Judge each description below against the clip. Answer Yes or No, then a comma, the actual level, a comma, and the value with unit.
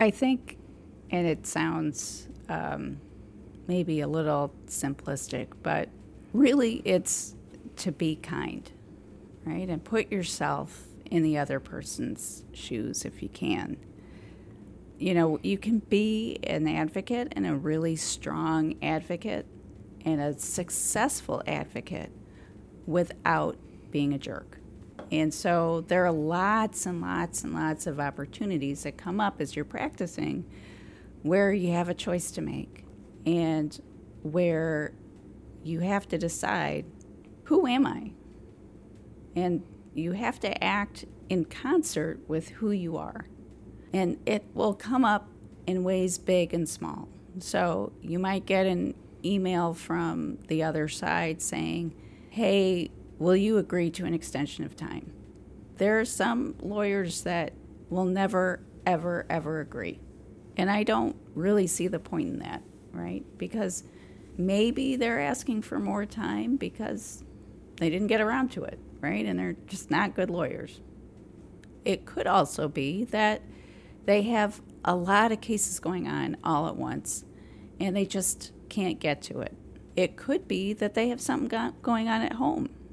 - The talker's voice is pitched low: No, medium, 170 Hz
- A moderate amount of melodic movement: No, wide, 5.9 semitones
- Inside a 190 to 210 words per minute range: No, average, 145 wpm